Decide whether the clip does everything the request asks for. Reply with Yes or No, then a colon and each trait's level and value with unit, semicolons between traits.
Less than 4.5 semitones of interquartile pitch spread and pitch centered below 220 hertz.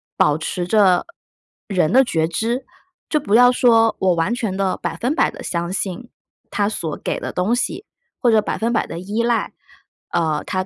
No: average, 4.9 semitones; high, 205 Hz